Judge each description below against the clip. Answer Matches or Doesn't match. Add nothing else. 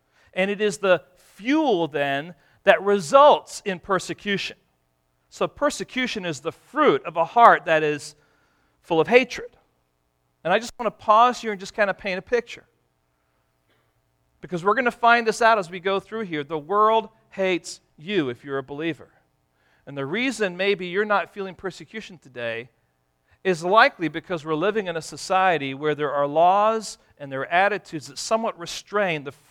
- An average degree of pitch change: Doesn't match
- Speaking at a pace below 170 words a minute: Doesn't match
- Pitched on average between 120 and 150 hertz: Doesn't match